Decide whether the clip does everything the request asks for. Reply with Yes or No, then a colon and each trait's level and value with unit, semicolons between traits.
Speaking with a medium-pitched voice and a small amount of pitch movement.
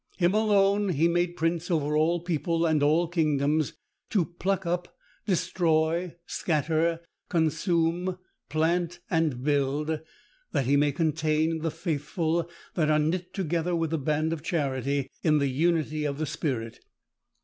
Yes: medium, 160 Hz; narrow, 2.3 semitones